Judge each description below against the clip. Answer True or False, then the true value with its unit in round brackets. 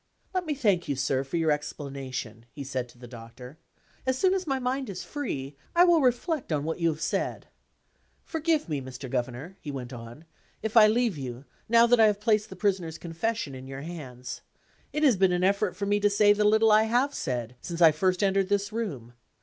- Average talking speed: False (215 wpm)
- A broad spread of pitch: True (8.7 semitones)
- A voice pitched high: False (180 Hz)